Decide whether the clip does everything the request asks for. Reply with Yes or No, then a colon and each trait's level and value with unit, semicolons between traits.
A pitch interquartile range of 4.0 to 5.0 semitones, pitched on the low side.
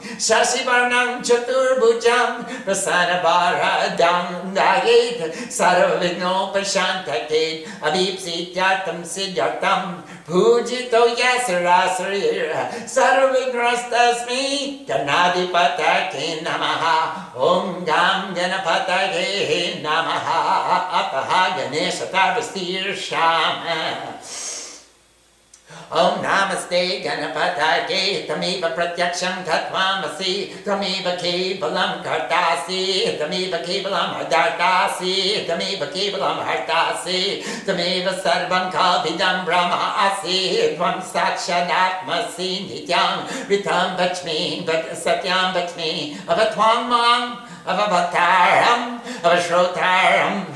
No: average, 4.7 semitones; medium, 185 Hz